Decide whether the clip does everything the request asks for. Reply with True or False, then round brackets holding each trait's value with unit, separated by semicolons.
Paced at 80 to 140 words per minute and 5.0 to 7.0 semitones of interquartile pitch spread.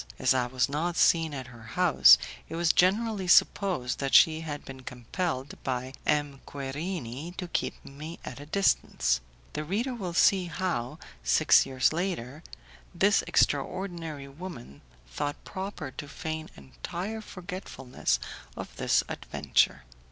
True (135 wpm; 5.6 semitones)